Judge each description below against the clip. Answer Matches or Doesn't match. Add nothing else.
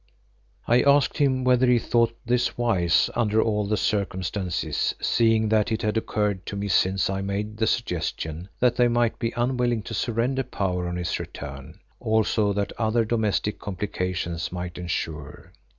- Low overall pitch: Matches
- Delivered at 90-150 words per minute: Doesn't match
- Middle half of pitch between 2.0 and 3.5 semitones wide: Doesn't match